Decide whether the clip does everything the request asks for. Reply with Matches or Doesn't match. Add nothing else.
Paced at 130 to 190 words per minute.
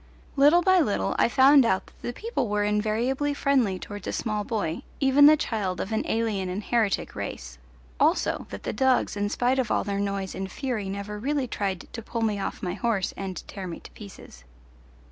Doesn't match